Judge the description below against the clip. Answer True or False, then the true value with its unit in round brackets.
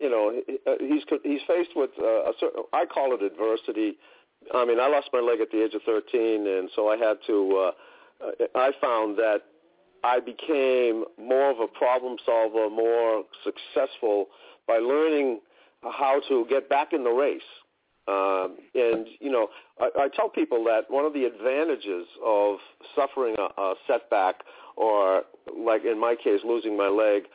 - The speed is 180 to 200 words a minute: False (165 wpm)